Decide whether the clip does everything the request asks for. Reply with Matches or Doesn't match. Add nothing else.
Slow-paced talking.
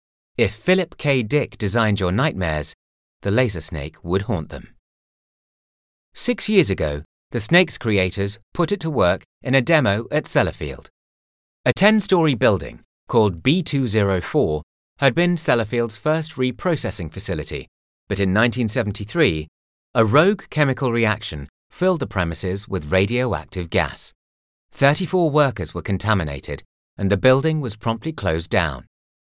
Matches